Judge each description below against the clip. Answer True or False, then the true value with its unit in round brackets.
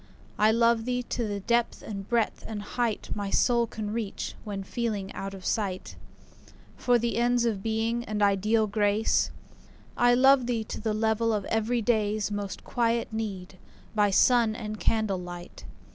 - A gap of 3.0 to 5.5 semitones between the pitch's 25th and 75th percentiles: False (2.4 semitones)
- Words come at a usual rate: True (160 wpm)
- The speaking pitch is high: True (220 Hz)